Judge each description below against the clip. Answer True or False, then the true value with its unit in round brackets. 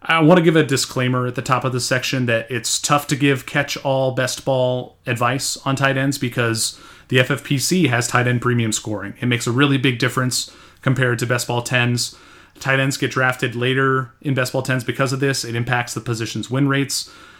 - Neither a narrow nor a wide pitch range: False (1.9 semitones)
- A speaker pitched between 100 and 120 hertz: False (130 Hz)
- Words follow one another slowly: False (215 wpm)